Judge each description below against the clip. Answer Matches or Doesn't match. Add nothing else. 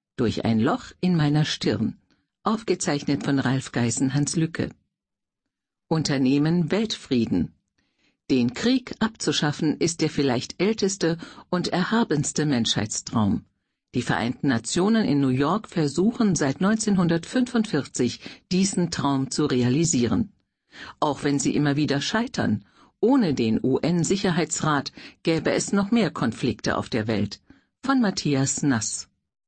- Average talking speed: Doesn't match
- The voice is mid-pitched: Matches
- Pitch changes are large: Matches